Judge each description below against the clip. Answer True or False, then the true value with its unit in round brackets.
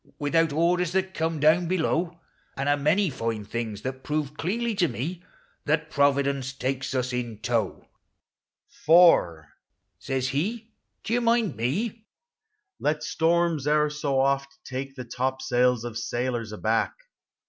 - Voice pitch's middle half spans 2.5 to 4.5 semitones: False (5.1 semitones)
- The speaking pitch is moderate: True (145 Hz)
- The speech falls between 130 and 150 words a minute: True (145 wpm)